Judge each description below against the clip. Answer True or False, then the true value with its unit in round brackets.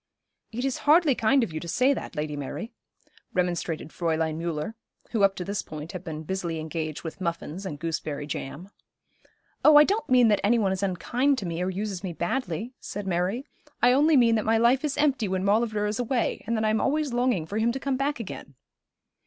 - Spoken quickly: True (215 wpm)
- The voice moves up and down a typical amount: False (6.5 semitones)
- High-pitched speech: True (205 Hz)